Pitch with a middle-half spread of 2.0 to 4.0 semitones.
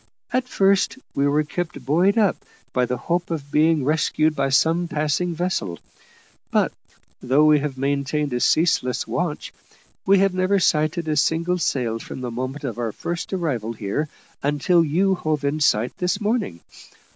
No: average, 4.4 semitones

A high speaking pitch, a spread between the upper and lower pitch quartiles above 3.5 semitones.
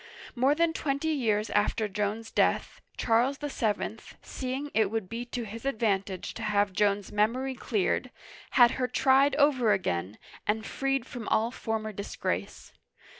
Yes: high, 225 Hz; average, 4.2 semitones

